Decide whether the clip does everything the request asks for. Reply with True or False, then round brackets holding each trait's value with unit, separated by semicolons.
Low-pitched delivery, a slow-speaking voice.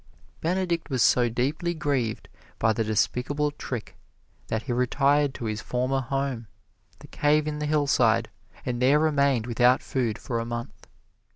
False (130 Hz; 155 wpm)